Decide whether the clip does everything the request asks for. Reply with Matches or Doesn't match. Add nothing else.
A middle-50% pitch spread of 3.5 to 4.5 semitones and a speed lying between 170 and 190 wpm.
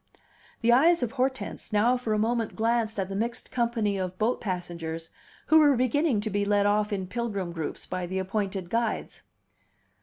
Matches